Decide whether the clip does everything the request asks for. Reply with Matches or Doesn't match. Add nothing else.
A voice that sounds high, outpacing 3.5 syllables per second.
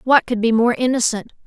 Matches